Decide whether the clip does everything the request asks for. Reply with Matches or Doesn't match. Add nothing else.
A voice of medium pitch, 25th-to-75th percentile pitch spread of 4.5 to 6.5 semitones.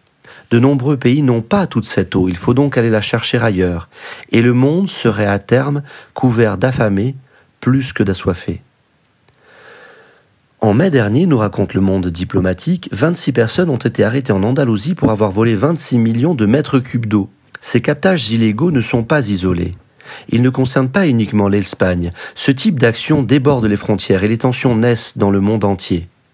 Doesn't match